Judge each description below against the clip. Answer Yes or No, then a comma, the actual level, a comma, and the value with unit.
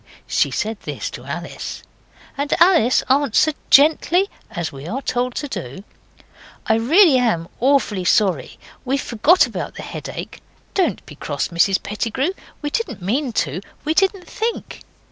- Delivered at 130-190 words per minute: Yes, average, 145 wpm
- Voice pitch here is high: Yes, very high, 255 Hz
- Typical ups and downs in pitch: No, wide, 7.1 semitones